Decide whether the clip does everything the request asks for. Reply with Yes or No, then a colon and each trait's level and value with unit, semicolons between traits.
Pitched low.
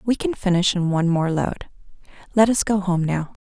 No: high, 190 Hz